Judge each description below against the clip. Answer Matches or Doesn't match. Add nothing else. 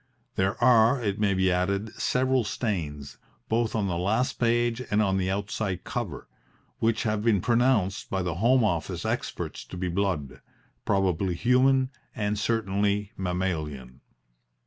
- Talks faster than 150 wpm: Doesn't match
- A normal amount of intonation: Matches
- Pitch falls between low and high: Doesn't match